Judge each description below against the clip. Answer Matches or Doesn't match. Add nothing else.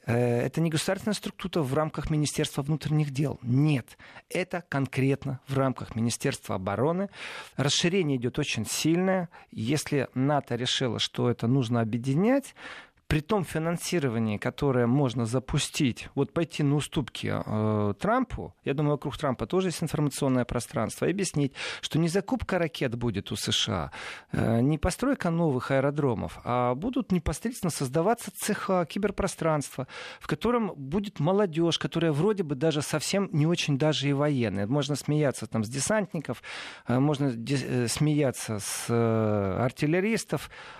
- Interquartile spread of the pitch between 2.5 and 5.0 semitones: Doesn't match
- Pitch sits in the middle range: Matches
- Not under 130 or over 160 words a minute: Matches